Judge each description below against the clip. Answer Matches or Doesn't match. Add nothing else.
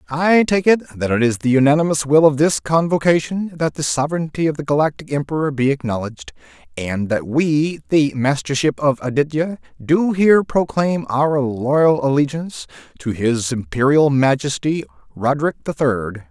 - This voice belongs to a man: Matches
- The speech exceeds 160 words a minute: Doesn't match